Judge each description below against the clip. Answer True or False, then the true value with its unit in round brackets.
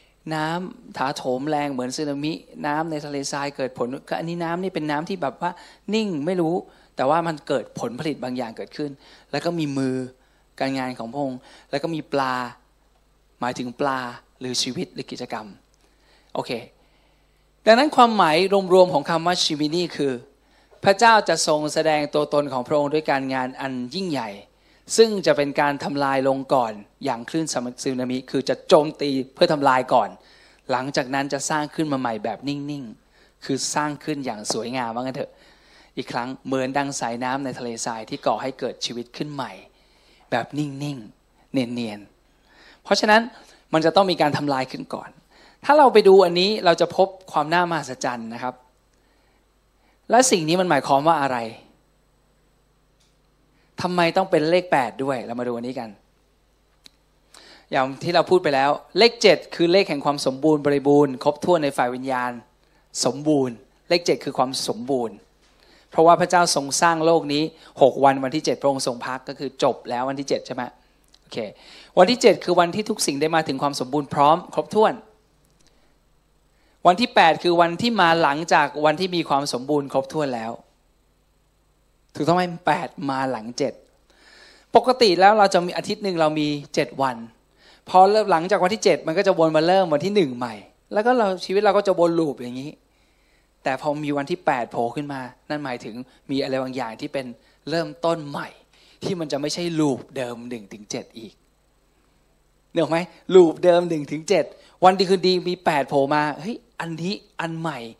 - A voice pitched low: False (150 Hz)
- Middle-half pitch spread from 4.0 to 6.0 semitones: True (4.7 semitones)